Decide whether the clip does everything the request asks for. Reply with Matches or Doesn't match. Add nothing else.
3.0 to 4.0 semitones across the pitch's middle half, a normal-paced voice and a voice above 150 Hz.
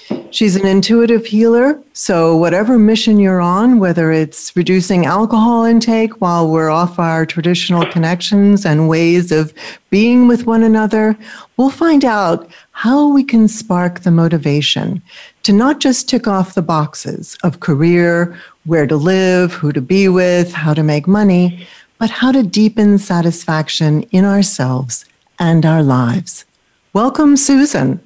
Doesn't match